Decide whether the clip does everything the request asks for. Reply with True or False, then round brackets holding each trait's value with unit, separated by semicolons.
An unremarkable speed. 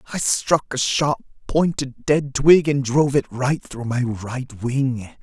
True (170 wpm)